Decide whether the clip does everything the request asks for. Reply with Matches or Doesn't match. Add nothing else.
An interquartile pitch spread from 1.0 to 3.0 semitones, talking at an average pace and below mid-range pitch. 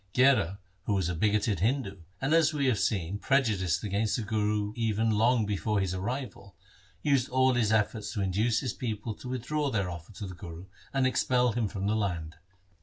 Doesn't match